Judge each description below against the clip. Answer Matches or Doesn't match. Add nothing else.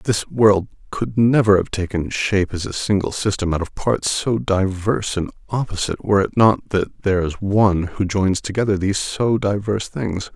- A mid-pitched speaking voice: Doesn't match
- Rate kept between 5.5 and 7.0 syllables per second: Doesn't match